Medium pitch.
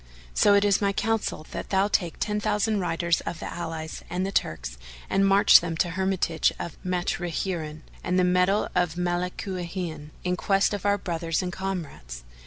Yes: medium, 180 Hz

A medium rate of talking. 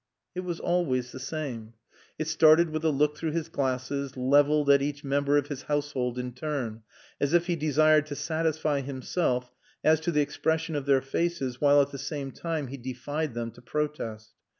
Yes: average, 190 wpm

